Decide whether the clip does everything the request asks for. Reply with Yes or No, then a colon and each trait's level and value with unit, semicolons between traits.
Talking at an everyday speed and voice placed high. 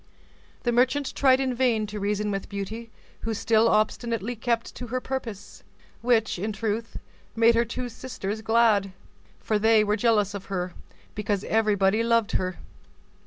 Yes: average, 155 wpm; high, 220 Hz